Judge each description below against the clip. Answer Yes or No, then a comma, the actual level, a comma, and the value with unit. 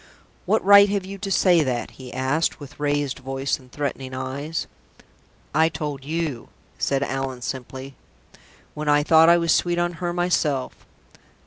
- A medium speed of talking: Yes, average, 155 wpm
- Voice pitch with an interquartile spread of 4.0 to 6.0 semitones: Yes, average, 4.3 semitones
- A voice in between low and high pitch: Yes, medium, 145 Hz